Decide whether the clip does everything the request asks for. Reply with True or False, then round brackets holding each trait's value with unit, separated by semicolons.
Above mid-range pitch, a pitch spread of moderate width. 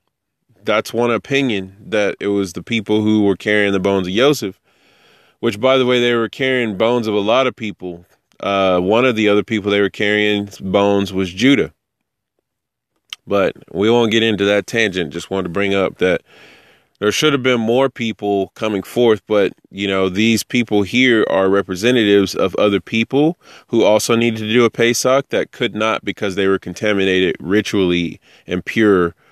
False (105 Hz; 3.0 semitones)